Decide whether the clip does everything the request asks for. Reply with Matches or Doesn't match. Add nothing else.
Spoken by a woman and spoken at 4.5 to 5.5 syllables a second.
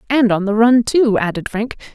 Matches